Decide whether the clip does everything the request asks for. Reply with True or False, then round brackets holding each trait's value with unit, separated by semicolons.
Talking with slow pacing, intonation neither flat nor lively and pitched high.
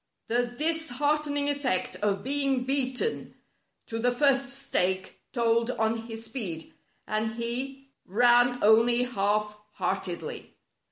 True (110 wpm; 3.7 semitones; 245 Hz)